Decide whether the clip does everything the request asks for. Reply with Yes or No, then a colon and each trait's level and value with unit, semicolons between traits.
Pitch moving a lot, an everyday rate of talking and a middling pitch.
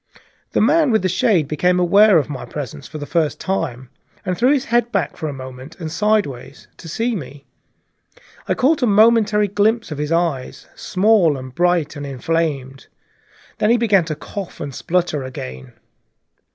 Yes: wide, 6.8 semitones; average, 175 wpm; medium, 170 Hz